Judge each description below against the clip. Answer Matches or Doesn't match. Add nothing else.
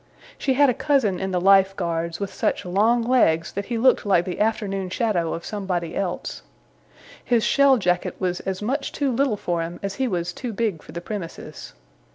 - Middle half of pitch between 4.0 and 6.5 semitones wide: Matches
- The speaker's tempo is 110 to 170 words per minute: Doesn't match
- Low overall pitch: Doesn't match